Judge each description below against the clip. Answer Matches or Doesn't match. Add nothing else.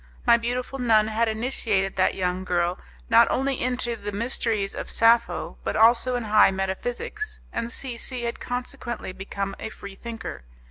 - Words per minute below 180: Matches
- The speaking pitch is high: Matches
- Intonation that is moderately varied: Matches